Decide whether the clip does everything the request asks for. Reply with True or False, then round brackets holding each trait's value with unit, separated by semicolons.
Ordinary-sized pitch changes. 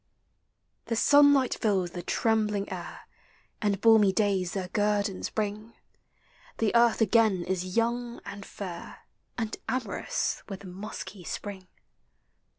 True (3.0 semitones)